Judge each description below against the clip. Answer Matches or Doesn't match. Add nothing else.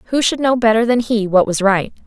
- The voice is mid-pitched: Doesn't match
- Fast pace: Matches